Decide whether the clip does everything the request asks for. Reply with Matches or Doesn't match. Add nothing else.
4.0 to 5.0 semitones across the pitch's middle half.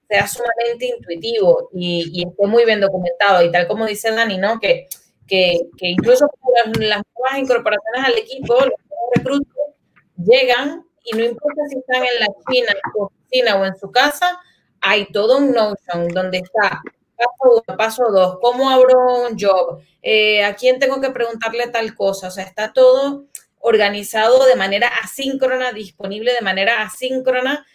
Matches